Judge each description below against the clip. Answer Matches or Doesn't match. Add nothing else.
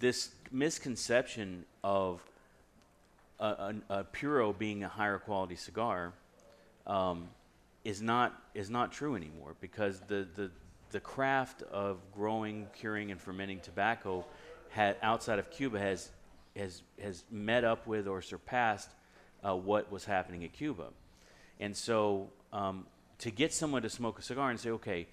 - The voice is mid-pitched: Doesn't match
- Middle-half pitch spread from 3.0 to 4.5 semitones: Matches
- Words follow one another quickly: Doesn't match